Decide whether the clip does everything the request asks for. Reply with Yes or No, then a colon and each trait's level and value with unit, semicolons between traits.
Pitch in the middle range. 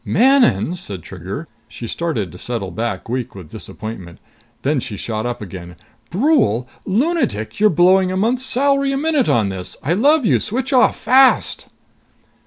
Yes: medium, 170 Hz